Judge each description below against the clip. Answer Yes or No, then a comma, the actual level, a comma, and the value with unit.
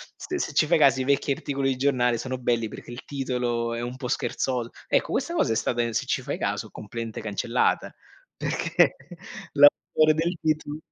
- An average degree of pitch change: Yes, average, 3.5 semitones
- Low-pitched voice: Yes, low, 130 Hz